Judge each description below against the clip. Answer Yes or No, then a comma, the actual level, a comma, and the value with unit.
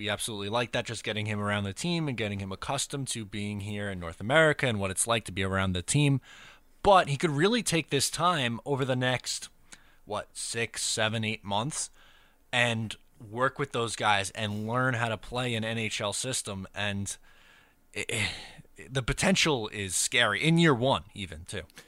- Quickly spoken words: No, average, 190 wpm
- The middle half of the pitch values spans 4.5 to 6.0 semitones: Yes, average, 4.9 semitones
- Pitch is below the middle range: Yes, low, 115 Hz